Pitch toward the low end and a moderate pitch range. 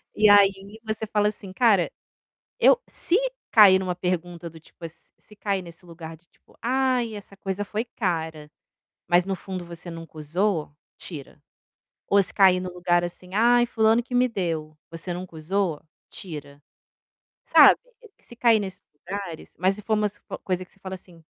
No: medium, 185 Hz; average, 3.6 semitones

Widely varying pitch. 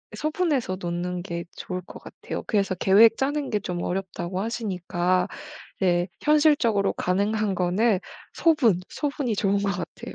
No: average, 4.5 semitones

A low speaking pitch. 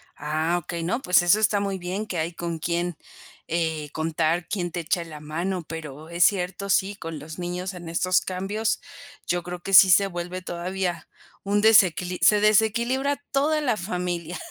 No: medium, 180 Hz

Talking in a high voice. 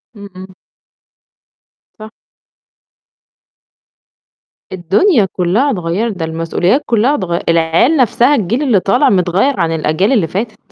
Yes: high, 195 Hz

